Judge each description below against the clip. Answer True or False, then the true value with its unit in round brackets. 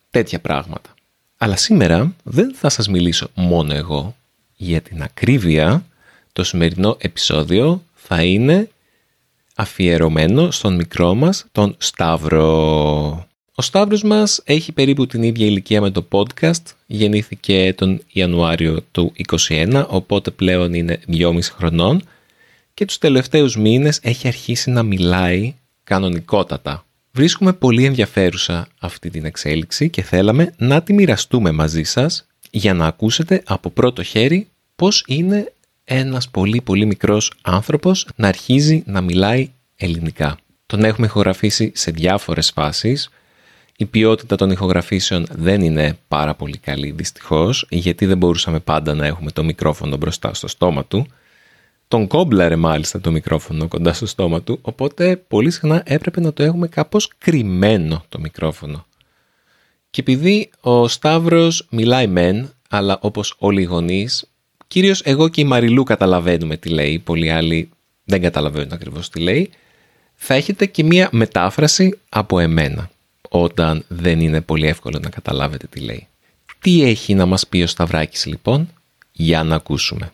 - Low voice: True (100 Hz)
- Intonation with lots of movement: True (7.9 semitones)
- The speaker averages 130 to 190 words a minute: True (140 wpm)